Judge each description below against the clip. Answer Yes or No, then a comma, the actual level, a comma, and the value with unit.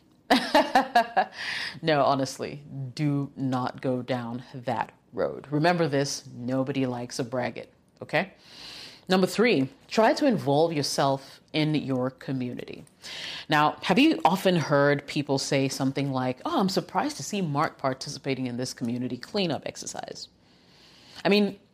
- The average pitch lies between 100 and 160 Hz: Yes, medium, 140 Hz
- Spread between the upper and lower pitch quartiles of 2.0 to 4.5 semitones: No, average, 5.2 semitones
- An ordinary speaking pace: No, slow, 130 wpm